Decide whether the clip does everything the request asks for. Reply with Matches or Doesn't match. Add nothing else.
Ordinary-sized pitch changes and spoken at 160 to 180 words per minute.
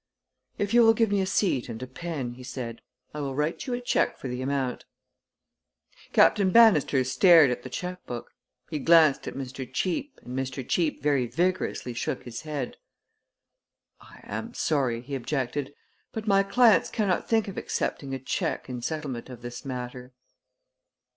Doesn't match